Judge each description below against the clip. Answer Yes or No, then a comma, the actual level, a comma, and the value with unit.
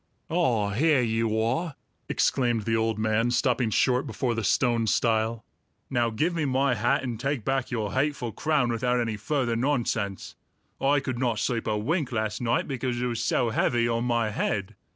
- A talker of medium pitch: No, low, 120 Hz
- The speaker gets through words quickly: No, average, 180 wpm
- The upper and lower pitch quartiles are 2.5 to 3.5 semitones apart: Yes, average, 2.8 semitones